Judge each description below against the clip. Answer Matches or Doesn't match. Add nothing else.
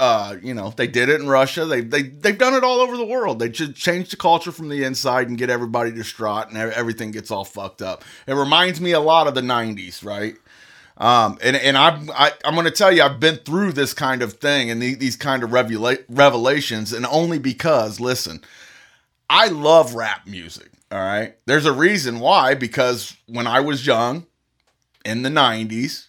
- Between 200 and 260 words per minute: Matches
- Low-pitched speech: Matches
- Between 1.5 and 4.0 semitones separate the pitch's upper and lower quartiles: Doesn't match